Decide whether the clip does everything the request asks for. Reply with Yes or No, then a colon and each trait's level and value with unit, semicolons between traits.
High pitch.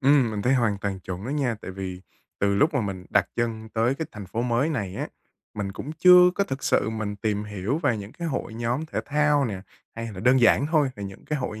No: low, 115 Hz